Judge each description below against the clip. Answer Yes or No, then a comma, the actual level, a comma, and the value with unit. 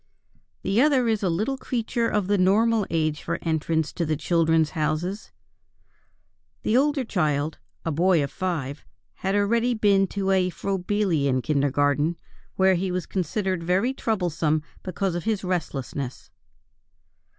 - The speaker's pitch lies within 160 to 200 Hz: Yes, medium, 185 Hz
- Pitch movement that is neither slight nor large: Yes, average, 4.6 semitones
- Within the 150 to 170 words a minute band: No, average, 140 wpm